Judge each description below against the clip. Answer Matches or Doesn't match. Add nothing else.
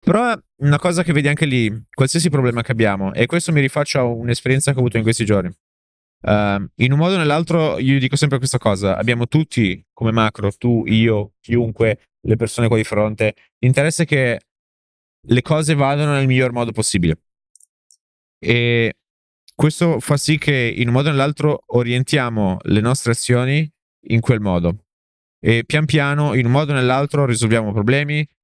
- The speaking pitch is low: Matches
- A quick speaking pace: Matches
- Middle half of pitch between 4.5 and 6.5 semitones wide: Matches